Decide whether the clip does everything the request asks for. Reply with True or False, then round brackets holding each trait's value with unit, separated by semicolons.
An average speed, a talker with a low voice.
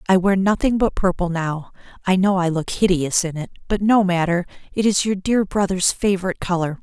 False (195 wpm; 185 Hz)